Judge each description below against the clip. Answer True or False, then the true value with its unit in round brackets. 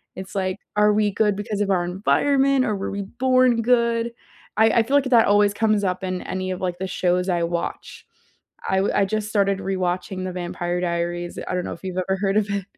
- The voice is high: True (195 Hz)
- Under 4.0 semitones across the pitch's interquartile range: True (2.8 semitones)